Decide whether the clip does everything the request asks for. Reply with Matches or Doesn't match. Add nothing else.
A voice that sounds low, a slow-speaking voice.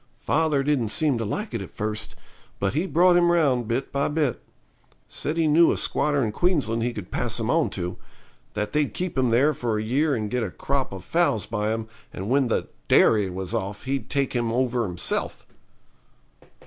Doesn't match